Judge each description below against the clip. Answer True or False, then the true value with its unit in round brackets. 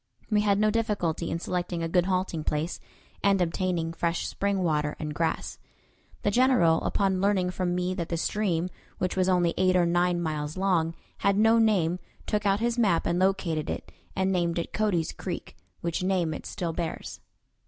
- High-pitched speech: False (180 Hz)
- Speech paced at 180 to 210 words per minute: True (185 wpm)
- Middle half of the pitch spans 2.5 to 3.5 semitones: True (2.8 semitones)